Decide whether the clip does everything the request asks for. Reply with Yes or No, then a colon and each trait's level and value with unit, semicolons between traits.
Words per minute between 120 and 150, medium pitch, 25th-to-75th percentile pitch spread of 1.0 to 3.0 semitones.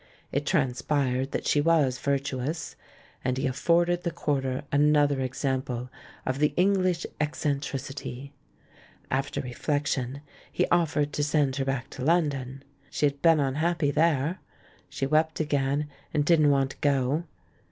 Yes: average, 140 wpm; medium, 145 Hz; narrow, 2.5 semitones